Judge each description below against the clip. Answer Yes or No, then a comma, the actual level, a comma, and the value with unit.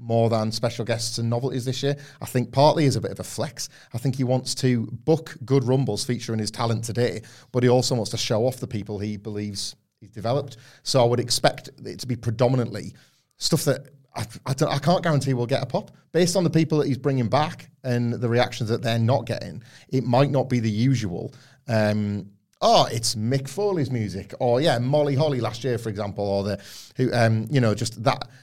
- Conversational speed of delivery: No, fast, 225 wpm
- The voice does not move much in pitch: No, average, 3.2 semitones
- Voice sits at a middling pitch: No, low, 125 Hz